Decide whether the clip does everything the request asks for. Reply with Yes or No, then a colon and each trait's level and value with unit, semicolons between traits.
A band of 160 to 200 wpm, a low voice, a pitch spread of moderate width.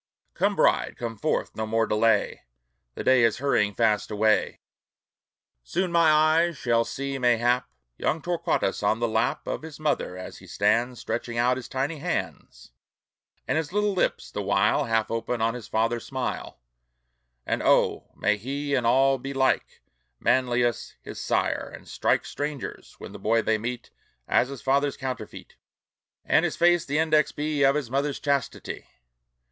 Yes: average, 165 wpm; low, 125 Hz; average, 4.1 semitones